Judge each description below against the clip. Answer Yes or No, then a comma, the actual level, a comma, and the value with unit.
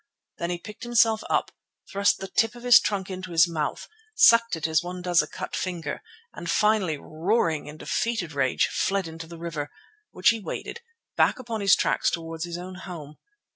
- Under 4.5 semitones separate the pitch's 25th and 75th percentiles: No, average, 4.8 semitones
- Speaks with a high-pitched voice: No, medium, 180 Hz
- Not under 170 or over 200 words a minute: Yes, average, 195 wpm